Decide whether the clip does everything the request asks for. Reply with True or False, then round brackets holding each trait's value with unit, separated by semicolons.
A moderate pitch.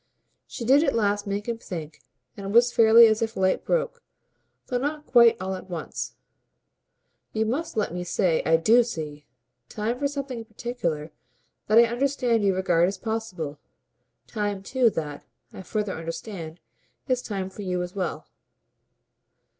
False (210 Hz)